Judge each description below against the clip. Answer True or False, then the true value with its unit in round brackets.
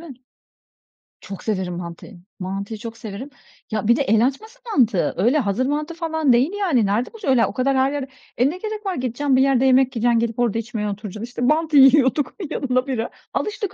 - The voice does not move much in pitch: False (4.5 semitones)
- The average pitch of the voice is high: True (255 Hz)